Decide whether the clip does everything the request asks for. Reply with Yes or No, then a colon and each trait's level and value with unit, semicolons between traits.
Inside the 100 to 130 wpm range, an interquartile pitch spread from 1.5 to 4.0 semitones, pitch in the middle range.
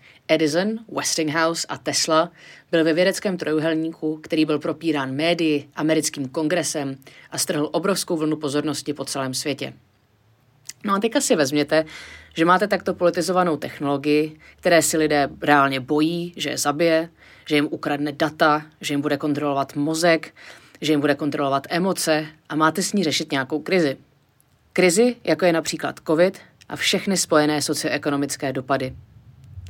No: average, 145 wpm; average, 2.7 semitones; medium, 155 Hz